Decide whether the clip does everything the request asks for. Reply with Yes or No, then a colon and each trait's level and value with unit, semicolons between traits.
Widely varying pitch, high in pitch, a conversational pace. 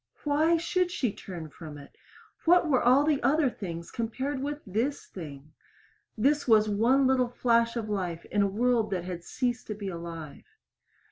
Yes: wide, 6.9 semitones; high, 230 Hz; average, 175 wpm